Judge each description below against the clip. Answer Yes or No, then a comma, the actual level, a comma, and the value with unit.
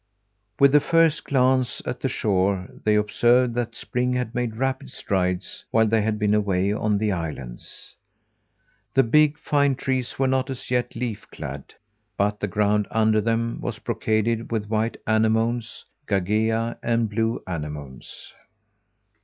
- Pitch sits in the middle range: No, low, 110 Hz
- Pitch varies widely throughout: No, average, 3.3 semitones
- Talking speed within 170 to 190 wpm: No, average, 145 wpm